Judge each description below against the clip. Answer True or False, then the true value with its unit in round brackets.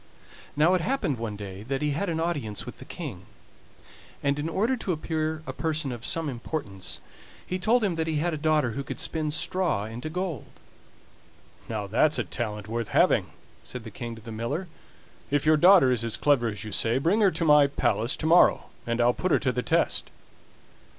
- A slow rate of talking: False (205 wpm)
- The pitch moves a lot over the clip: True (5.8 semitones)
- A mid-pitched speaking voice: True (145 Hz)